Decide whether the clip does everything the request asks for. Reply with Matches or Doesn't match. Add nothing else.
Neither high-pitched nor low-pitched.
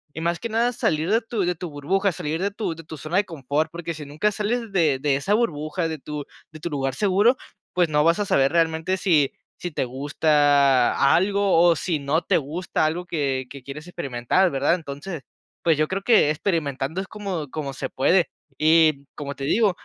Matches